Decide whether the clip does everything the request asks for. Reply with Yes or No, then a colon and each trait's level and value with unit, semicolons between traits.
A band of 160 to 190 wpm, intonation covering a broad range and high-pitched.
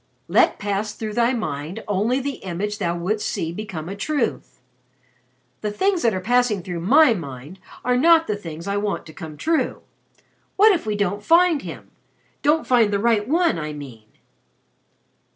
Yes: average, 170 wpm; wide, 6.2 semitones; high, 210 Hz